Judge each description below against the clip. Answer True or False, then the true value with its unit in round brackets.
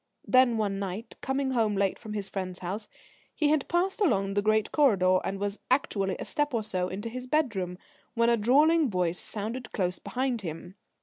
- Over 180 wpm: True (190 wpm)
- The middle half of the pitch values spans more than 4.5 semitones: True (5.0 semitones)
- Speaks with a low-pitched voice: False (215 Hz)